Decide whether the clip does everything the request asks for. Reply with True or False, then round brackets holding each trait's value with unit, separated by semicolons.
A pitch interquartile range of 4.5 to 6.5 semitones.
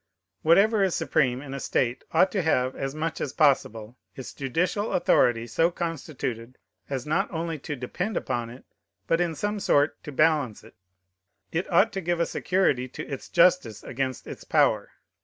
True (5.2 semitones)